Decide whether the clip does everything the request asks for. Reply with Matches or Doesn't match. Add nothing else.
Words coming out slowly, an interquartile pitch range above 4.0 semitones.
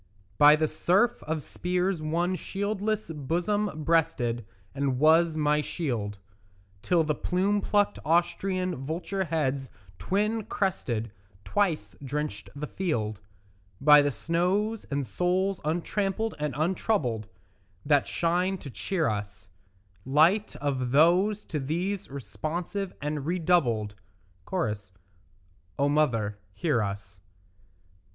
Matches